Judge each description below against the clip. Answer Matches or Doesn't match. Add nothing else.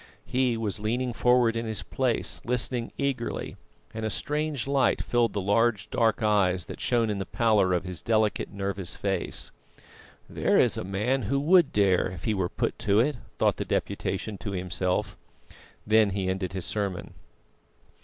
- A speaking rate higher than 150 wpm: Matches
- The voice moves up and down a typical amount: Matches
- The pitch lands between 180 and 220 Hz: Doesn't match